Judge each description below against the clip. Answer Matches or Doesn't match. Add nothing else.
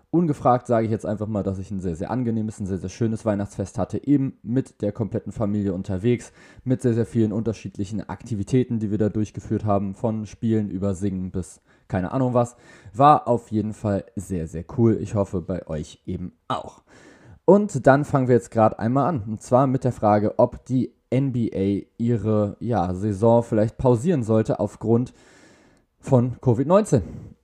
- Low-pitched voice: Matches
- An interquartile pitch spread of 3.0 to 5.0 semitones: Matches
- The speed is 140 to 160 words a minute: Doesn't match